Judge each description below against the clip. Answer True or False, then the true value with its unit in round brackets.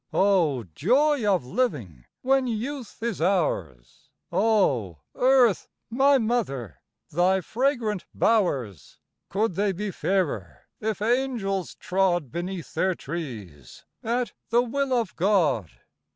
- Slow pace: True (110 wpm)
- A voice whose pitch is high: True (195 Hz)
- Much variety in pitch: True (8.3 semitones)